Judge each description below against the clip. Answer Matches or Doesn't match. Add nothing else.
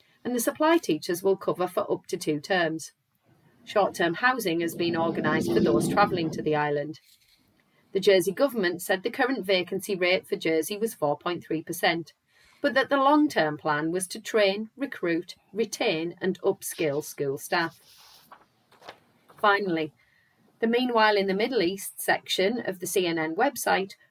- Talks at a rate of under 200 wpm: Matches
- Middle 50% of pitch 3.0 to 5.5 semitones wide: Matches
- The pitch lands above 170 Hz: Matches